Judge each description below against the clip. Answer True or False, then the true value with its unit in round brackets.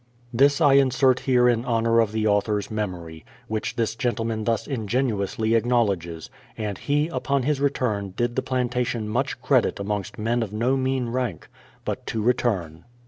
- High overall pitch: False (115 Hz)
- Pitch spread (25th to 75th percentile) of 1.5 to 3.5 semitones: True (3.2 semitones)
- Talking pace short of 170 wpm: True (160 wpm)